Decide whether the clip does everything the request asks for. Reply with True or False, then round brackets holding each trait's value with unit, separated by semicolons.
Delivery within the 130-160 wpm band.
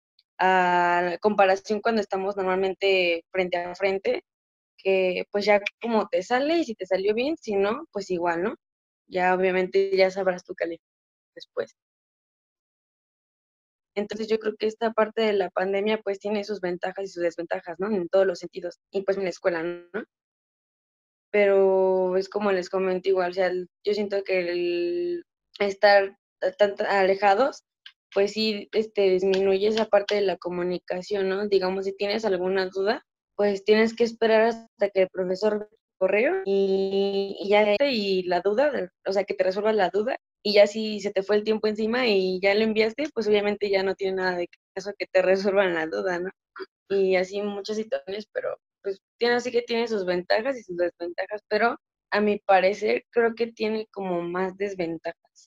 False (175 wpm)